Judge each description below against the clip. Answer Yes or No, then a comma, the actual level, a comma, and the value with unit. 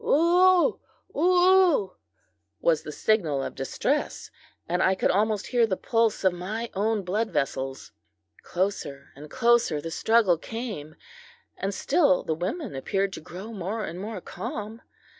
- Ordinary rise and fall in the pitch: Yes, average, 4.8 semitones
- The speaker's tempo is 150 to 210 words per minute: No, average, 140 wpm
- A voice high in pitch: Yes, high, 205 Hz